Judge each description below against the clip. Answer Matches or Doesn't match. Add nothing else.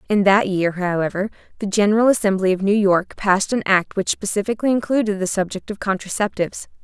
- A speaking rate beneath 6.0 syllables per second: Doesn't match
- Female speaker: Matches